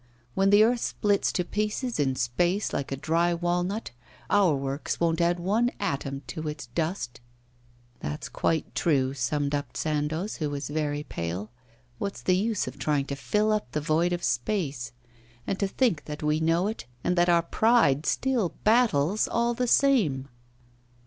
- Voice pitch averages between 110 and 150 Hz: No, medium, 170 Hz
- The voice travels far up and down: Yes, wide, 6.1 semitones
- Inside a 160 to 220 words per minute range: Yes, average, 170 wpm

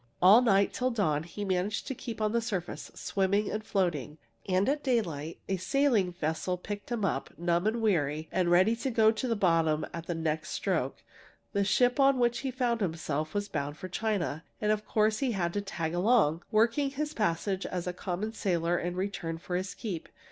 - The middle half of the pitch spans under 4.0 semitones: No, average, 4.7 semitones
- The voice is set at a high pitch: Yes, high, 195 Hz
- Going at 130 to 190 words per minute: No, average, 200 wpm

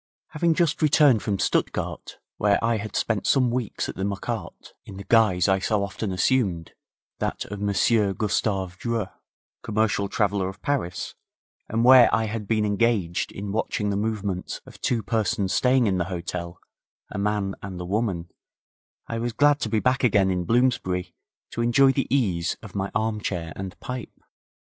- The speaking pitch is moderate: No, low, 105 Hz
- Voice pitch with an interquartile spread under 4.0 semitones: Yes, average, 3.4 semitones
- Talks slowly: No, average, 170 wpm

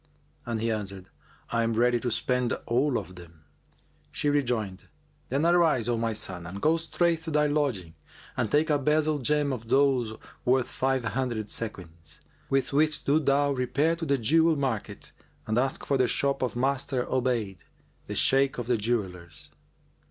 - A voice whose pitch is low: Yes, low, 125 Hz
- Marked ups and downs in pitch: No, average, 4.6 semitones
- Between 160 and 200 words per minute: Yes, average, 170 wpm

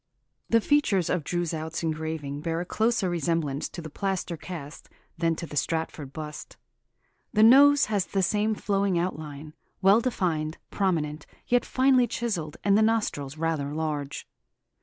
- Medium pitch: Yes, medium, 170 Hz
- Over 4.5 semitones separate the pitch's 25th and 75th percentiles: Yes, average, 5.0 semitones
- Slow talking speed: No, average, 145 wpm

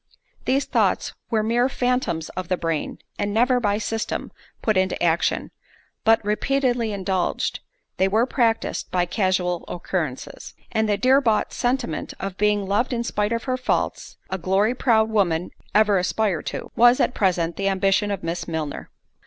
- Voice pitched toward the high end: Yes, high, 205 Hz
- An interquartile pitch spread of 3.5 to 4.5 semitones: Yes, average, 4.1 semitones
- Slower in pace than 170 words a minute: Yes, average, 160 wpm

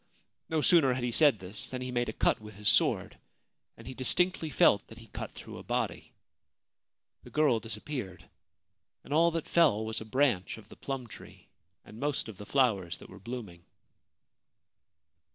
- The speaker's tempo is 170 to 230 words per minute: Yes, average, 180 wpm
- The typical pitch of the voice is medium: No, low, 120 Hz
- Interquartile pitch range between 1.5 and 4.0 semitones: No, average, 5.2 semitones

